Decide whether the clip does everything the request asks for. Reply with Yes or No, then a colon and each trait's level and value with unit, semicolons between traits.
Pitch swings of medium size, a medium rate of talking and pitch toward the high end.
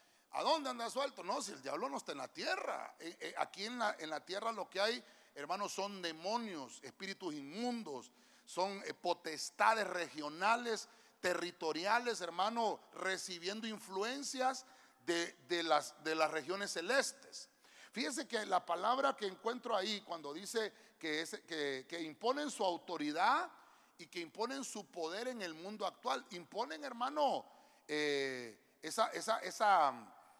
No: wide, 5.8 semitones; average, 140 wpm; high, 200 Hz